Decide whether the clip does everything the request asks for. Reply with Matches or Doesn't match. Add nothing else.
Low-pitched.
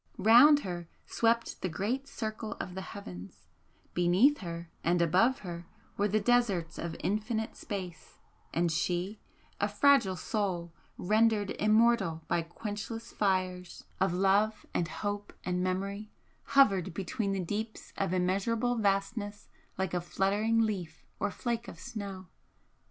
Doesn't match